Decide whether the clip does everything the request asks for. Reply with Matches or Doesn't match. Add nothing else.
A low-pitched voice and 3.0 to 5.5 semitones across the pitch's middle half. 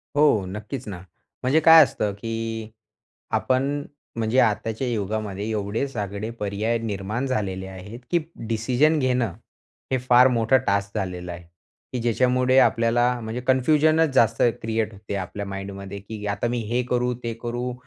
Matches